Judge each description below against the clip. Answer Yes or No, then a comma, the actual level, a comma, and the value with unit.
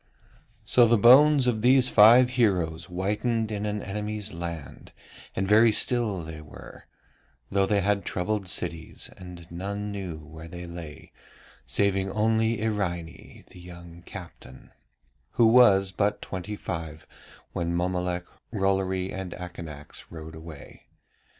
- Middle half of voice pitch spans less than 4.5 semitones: Yes, average, 3.7 semitones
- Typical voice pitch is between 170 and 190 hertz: No, very low, 95 Hz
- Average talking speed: No, slow, 130 wpm